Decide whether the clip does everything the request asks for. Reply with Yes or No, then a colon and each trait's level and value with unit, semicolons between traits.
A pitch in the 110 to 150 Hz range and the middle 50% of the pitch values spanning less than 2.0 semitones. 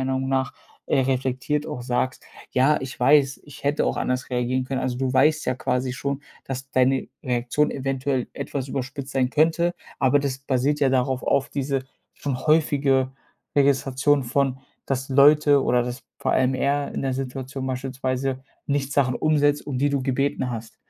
Yes: low, 135 Hz; narrow, 1.6 semitones